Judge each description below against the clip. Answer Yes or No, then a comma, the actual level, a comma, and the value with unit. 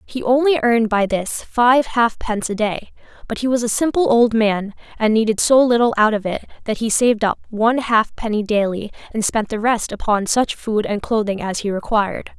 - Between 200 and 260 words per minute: Yes, fast, 205 wpm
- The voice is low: No, high, 225 Hz